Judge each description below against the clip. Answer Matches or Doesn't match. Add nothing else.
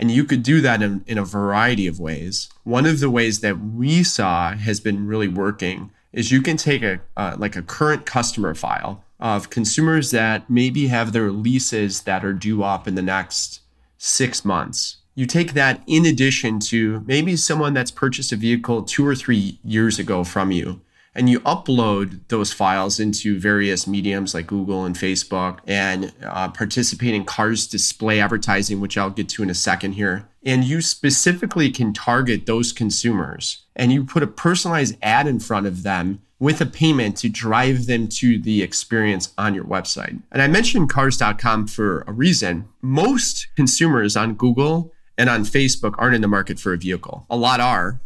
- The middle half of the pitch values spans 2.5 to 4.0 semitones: Doesn't match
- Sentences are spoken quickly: Doesn't match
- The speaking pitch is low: Matches